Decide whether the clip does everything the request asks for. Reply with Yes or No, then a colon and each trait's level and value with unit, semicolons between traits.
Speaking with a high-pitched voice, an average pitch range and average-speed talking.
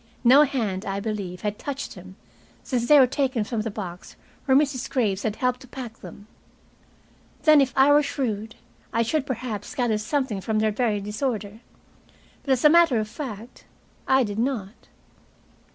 Yes: high, 235 Hz; average, 4.2 semitones; average, 170 wpm